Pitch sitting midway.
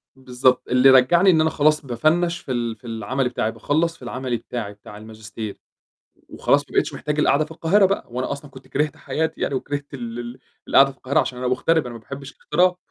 No: low, 130 Hz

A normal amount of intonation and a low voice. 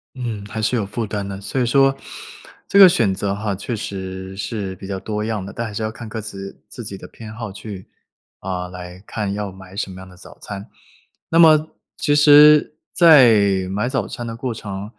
Yes: average, 3.6 semitones; low, 105 Hz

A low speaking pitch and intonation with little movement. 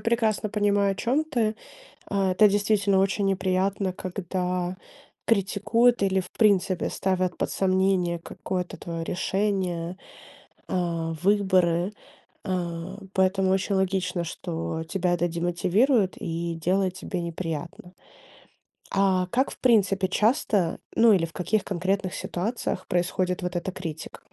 No: medium, 185 Hz; narrow, 2.2 semitones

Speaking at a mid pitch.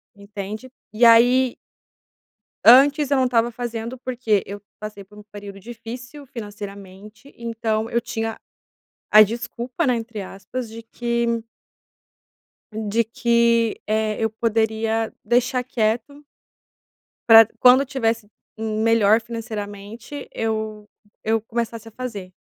No: high, 225 Hz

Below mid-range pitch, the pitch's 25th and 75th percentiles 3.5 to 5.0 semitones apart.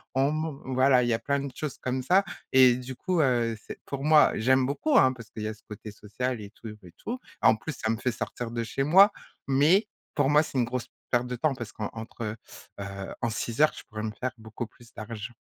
Yes: low, 125 Hz; average, 3.8 semitones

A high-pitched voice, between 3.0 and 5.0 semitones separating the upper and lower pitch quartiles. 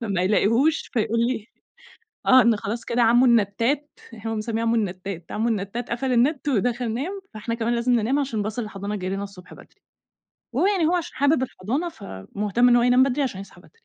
Yes: high, 230 Hz; average, 3.7 semitones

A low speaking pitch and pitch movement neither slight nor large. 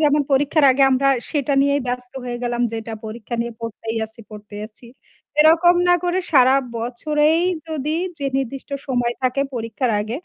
No: very high, 255 Hz; average, 3.8 semitones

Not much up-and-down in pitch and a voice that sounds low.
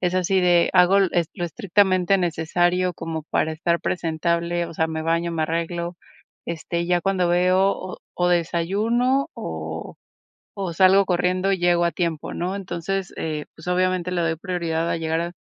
No: narrow, 1.8 semitones; medium, 175 Hz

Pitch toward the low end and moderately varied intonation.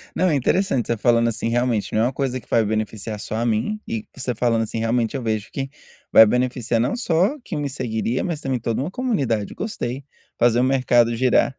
Yes: low, 120 Hz; average, 3.2 semitones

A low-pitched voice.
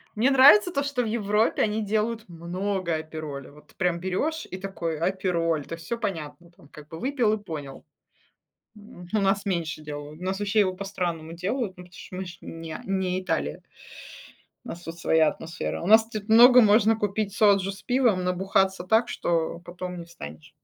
No: medium, 185 Hz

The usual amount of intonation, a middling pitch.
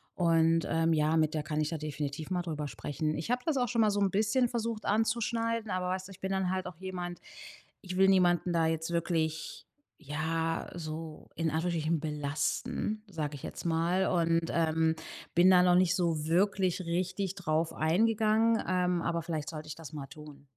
Yes: average, 3.1 semitones; medium, 170 Hz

